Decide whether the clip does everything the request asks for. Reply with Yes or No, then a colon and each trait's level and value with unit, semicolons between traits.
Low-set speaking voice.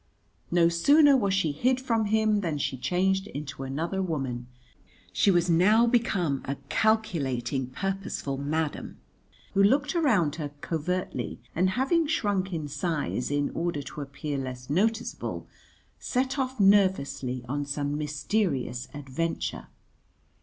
No: medium, 170 Hz